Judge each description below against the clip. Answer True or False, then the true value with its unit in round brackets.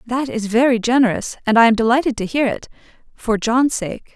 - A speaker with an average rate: True (190 wpm)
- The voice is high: True (235 Hz)